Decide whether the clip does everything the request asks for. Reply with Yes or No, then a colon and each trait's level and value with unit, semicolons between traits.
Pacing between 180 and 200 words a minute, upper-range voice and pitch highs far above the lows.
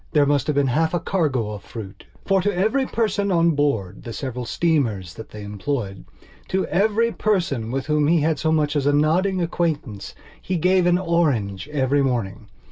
No: average, 185 wpm; medium, 150 Hz; wide, 6.5 semitones